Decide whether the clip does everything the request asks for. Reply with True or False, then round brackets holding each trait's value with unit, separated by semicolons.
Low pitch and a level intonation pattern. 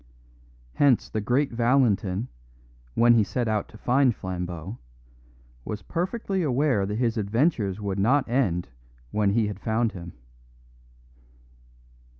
False (110 Hz; 4.3 semitones)